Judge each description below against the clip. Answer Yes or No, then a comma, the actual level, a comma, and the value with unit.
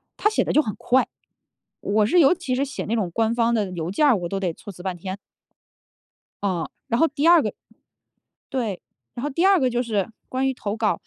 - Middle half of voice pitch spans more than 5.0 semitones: Yes, wide, 5.6 semitones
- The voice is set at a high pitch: Yes, high, 230 Hz